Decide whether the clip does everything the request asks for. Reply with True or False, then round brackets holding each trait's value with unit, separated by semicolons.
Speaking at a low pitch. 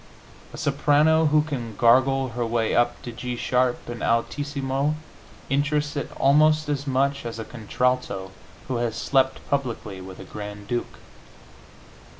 True (130 Hz)